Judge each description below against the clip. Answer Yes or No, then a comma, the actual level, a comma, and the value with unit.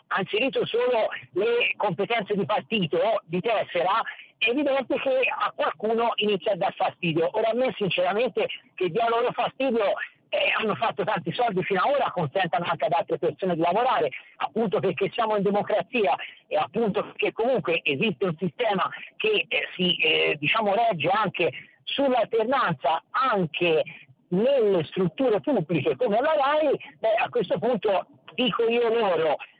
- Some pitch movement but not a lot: No, wide, 6.6 semitones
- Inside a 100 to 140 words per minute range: No, average, 155 wpm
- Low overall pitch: No, high, 220 Hz